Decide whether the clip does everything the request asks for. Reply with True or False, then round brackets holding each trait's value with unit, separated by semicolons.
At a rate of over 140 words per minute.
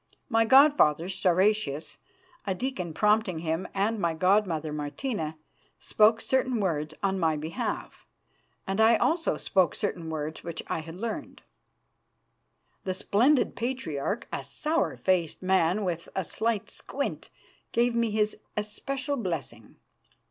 False (135 wpm)